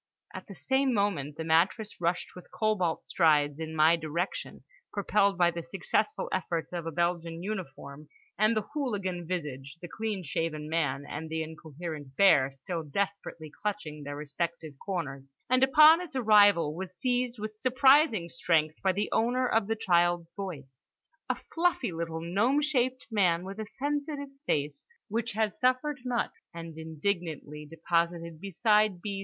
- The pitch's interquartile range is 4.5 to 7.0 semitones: Yes, average, 5.2 semitones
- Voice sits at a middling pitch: Yes, medium, 175 Hz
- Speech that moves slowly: No, average, 150 wpm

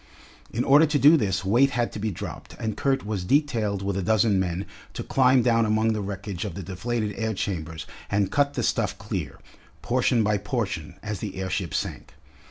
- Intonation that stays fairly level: No, average, 3.7 semitones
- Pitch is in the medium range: No, low, 105 Hz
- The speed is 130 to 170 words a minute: No, average, 195 wpm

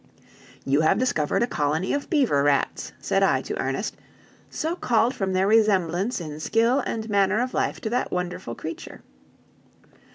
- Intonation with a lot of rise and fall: Yes, wide, 6.9 semitones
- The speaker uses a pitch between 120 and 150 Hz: No, high, 195 Hz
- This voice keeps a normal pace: Yes, average, 160 wpm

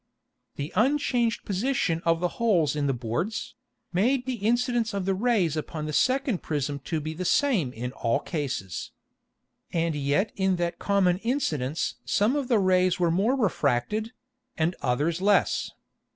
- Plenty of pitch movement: Yes, wide, 6.8 semitones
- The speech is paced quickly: No, average, 155 wpm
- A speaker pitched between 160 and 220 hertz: Yes, medium, 185 Hz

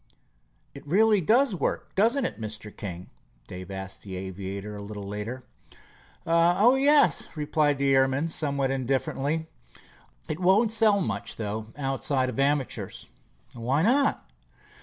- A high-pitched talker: No, medium, 140 Hz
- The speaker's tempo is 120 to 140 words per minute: Yes, slow, 135 wpm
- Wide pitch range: Yes, wide, 8.9 semitones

